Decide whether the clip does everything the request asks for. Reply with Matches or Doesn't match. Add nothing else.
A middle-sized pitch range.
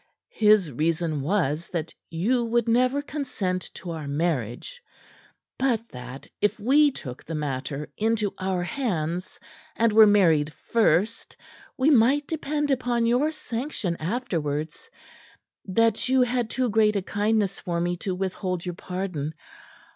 Doesn't match